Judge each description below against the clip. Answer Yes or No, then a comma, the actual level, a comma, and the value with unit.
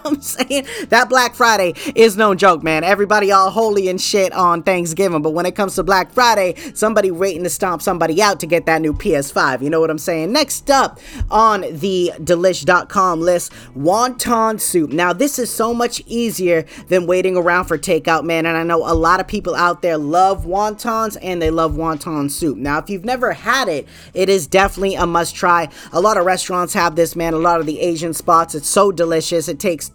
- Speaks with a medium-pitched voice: Yes, medium, 180 Hz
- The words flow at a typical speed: No, fast, 210 wpm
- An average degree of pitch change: Yes, average, 4.1 semitones